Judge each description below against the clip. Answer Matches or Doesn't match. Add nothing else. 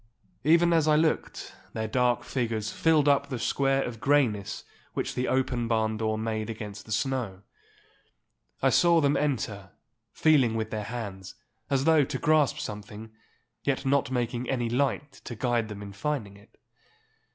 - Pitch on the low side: Matches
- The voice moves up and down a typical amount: Matches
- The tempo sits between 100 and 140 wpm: Doesn't match